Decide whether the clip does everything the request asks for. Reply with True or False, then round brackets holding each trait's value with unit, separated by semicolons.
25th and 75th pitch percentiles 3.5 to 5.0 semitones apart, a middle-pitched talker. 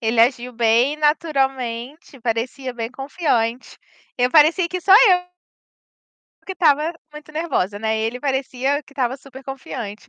False (4.2 semitones; 265 Hz)